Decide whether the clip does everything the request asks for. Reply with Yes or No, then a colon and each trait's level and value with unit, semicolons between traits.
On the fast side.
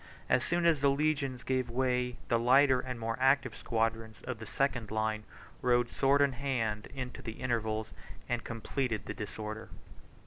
No: average, 165 wpm